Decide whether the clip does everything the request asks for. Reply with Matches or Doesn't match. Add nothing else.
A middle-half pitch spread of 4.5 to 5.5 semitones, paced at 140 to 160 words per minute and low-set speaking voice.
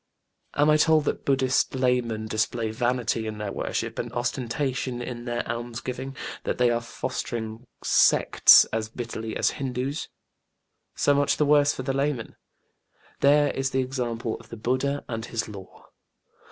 Doesn't match